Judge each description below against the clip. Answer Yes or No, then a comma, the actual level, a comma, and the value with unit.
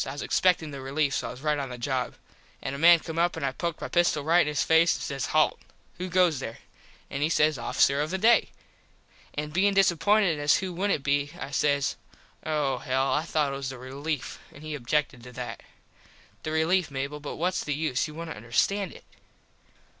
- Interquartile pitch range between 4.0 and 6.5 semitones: No, average, 3.4 semitones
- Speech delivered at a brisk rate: Yes, fast, 215 wpm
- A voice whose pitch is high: No, medium, 150 Hz